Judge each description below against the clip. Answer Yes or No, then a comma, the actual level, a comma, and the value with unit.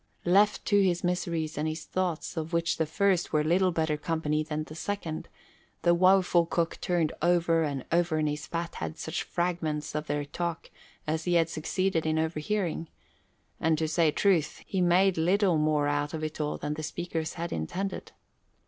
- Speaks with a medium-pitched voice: Yes, medium, 165 Hz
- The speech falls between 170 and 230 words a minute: Yes, average, 185 wpm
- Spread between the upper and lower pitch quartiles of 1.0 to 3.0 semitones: Yes, narrow, 2.4 semitones